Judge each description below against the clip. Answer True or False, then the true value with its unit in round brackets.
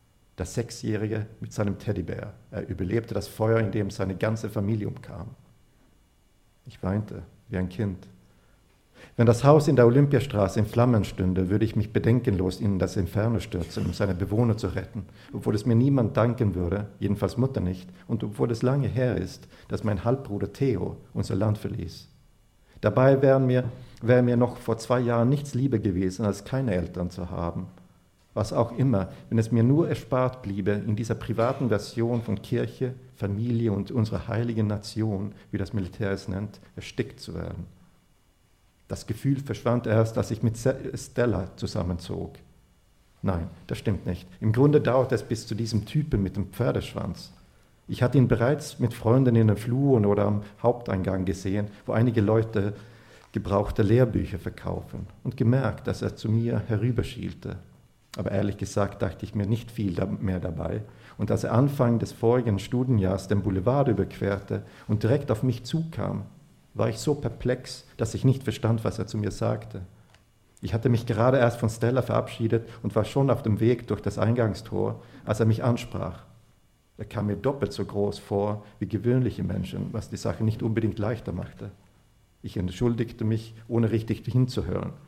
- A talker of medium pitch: False (110 Hz)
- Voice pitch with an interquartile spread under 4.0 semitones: True (3.1 semitones)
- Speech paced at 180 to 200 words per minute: False (170 wpm)